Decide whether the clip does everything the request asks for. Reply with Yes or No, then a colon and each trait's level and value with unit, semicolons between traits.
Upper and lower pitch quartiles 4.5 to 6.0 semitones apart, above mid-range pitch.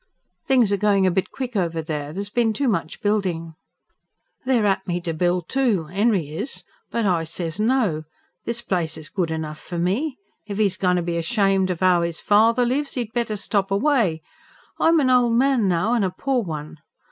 Yes: wide, 5.5 semitones; high, 195 Hz